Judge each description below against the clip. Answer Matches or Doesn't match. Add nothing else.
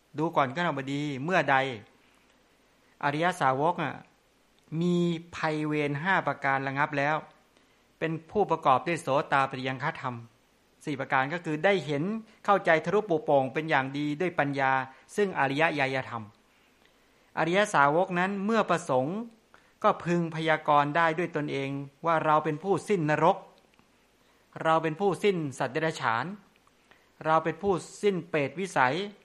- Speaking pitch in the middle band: Matches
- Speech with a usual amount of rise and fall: Matches